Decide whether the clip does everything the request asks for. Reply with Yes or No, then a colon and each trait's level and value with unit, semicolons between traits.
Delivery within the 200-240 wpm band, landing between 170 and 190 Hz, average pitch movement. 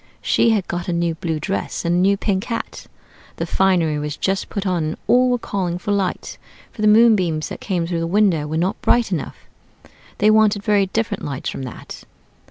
Yes: fast, 205 wpm; medium, 185 Hz; average, 3.9 semitones